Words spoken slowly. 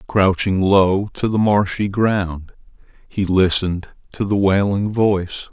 Yes: slow, 130 wpm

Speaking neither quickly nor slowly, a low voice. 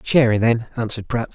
Yes: average, 180 wpm; low, 115 Hz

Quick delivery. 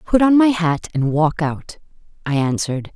No: average, 185 wpm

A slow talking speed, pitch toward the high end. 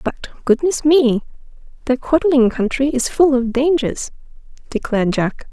Yes: slow, 110 wpm; very high, 265 Hz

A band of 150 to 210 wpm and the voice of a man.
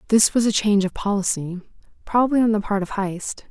No: fast, 205 wpm; female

